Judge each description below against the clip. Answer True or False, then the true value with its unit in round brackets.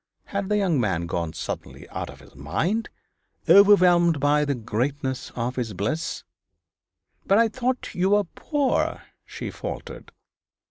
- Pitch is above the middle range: False (155 Hz)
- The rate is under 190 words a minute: True (140 wpm)